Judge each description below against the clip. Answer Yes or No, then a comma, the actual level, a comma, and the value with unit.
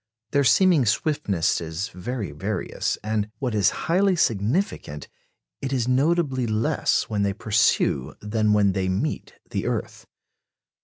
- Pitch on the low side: Yes, low, 110 Hz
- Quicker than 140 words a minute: No, slow, 135 wpm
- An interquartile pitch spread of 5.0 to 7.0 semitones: Yes, wide, 5.4 semitones